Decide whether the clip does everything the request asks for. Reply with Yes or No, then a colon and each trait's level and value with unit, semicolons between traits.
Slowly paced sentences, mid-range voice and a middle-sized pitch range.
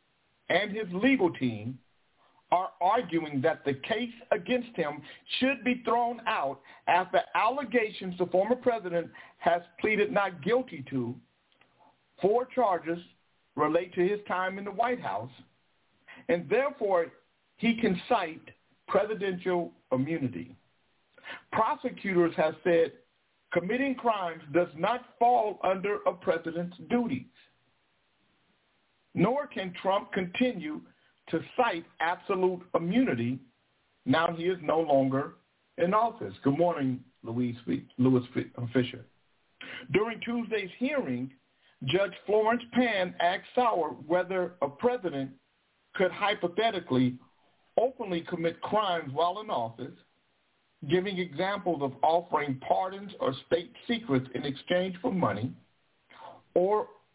No: slow, 110 wpm; medium, 180 Hz; wide, 6.9 semitones